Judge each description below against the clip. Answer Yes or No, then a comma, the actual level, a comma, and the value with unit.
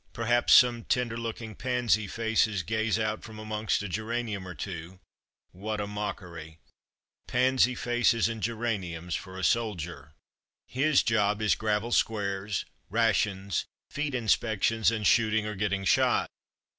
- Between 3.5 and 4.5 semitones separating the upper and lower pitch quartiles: No, average, 2.9 semitones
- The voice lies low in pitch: Yes, low, 110 Hz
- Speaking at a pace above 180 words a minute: No, average, 140 wpm